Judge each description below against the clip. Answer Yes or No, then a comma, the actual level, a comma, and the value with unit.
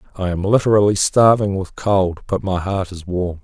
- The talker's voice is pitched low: Yes, very low, 95 Hz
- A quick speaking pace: No, average, 190 wpm